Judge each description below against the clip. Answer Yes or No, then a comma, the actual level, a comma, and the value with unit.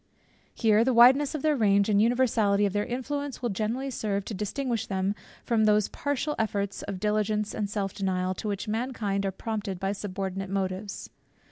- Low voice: No, high, 210 Hz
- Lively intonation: No, average, 3.2 semitones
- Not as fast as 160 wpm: No, average, 180 wpm